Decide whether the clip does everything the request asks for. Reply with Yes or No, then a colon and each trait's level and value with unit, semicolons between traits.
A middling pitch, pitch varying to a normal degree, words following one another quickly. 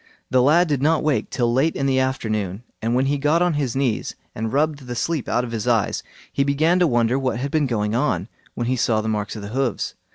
No: low, 130 Hz; average, 3.9 semitones; fast, 245 wpm